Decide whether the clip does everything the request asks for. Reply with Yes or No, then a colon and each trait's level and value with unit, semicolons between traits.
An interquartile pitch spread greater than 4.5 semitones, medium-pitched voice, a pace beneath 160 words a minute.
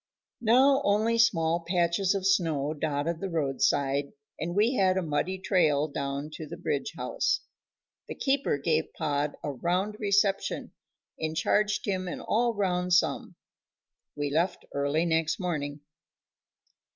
Yes: average, 4.9 semitones; medium, 170 Hz; average, 140 wpm